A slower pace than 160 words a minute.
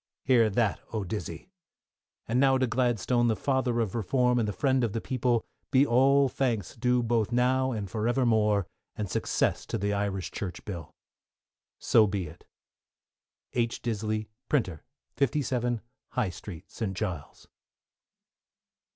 Yes: average, 140 wpm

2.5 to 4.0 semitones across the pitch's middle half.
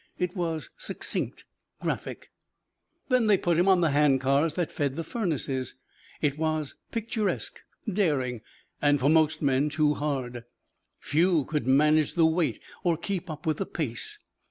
Yes: average, 3.5 semitones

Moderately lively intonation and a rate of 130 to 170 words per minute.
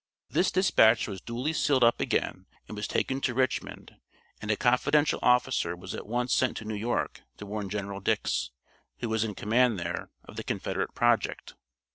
No: average, 3.4 semitones; average, 180 wpm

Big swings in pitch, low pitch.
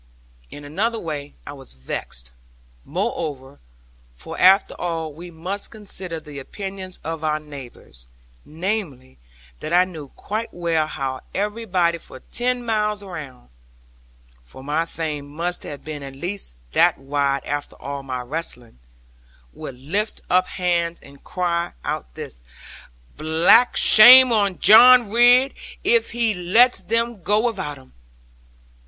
No: wide, 6.3 semitones; medium, 170 Hz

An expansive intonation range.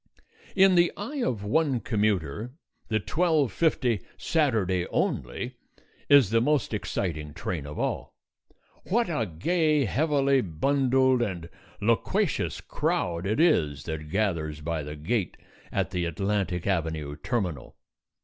Yes: wide, 8.9 semitones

